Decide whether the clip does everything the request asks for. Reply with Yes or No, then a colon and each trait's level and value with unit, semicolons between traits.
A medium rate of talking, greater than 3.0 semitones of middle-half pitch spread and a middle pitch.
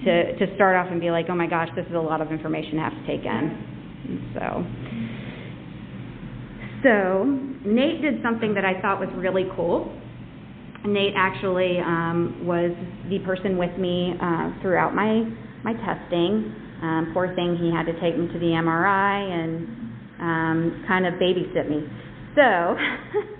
No: average, 165 wpm; average, 2.7 semitones; medium, 180 Hz